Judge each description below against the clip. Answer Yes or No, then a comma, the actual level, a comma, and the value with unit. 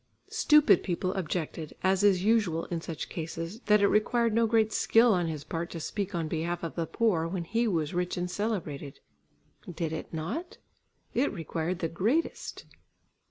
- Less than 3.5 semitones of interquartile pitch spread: No, average, 4.5 semitones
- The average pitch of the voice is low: No, medium, 180 Hz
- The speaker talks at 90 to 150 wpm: No, average, 170 wpm